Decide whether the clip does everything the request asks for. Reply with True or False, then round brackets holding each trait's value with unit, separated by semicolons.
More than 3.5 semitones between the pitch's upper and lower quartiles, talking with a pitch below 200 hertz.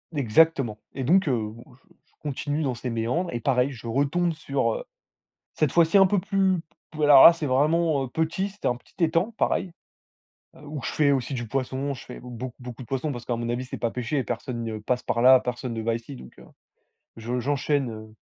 True (4.3 semitones; 135 Hz)